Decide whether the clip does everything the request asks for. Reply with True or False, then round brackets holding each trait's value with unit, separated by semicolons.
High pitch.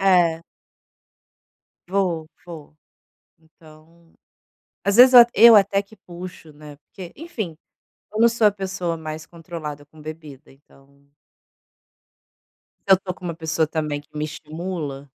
False (165 Hz)